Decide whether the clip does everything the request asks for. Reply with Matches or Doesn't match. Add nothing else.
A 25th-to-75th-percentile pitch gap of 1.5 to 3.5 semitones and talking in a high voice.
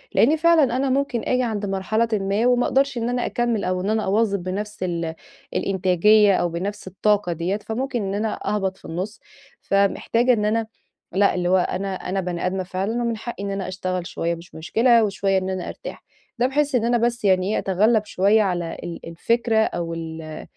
Doesn't match